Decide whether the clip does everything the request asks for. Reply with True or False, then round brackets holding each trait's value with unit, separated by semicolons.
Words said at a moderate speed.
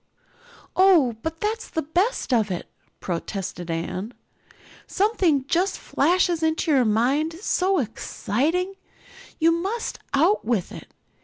False (125 wpm)